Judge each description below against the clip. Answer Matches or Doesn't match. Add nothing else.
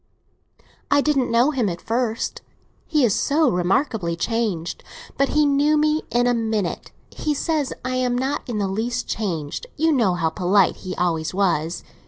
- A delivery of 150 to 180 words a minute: Matches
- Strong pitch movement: Matches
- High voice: Matches